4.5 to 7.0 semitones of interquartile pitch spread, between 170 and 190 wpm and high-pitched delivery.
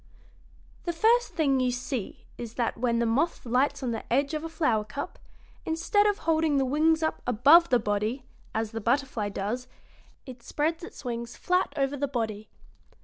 Yes: average, 5.2 semitones; average, 180 wpm; very high, 260 Hz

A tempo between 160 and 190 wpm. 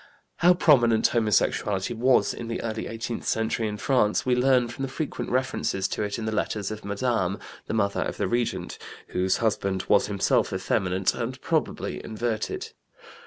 Yes: average, 165 wpm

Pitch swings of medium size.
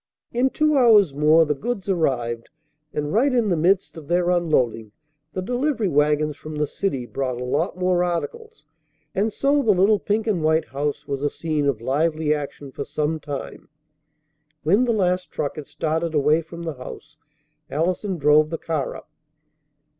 Yes: average, 4.5 semitones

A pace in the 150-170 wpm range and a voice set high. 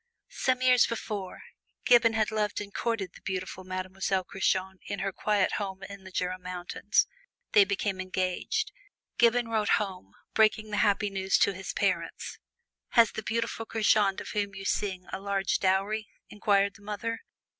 Yes: average, 160 wpm; high, 200 Hz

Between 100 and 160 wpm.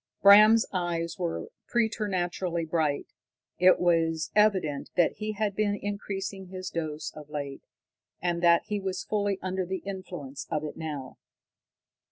Yes: average, 140 wpm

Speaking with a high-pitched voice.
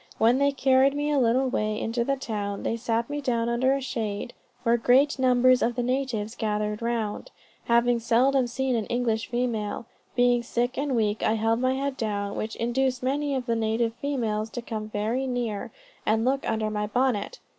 Yes: high, 240 Hz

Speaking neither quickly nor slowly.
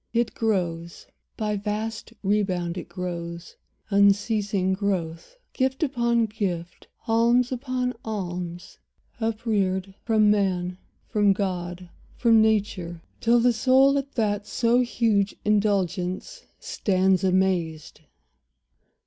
No: slow, 100 wpm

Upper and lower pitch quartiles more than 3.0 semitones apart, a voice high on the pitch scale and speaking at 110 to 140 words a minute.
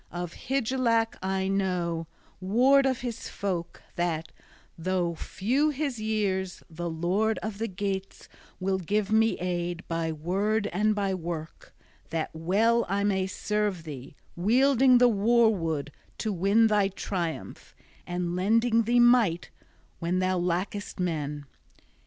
Yes: average, 4.2 semitones; high, 195 Hz; slow, 135 wpm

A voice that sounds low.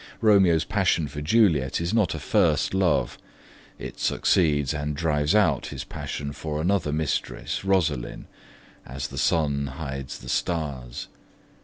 Yes: very low, 75 Hz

